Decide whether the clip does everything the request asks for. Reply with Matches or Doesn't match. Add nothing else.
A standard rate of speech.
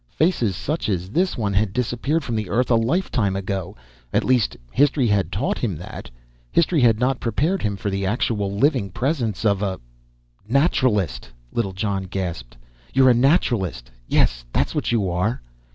Matches